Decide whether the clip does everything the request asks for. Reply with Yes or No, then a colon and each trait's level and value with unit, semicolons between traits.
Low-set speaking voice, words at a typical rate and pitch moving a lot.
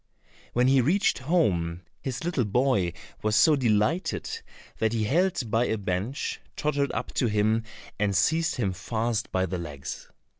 Yes: low, 115 Hz; average, 155 wpm; wide, 5.7 semitones